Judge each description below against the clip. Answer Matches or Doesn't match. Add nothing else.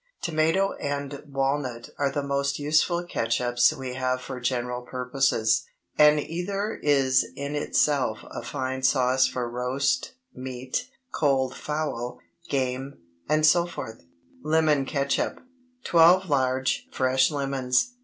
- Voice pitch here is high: Doesn't match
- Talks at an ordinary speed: Doesn't match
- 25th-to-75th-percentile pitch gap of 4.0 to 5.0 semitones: Doesn't match